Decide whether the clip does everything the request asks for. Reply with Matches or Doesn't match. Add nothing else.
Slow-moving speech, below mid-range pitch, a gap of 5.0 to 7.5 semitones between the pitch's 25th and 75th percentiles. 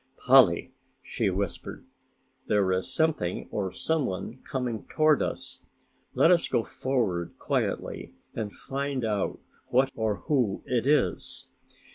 Matches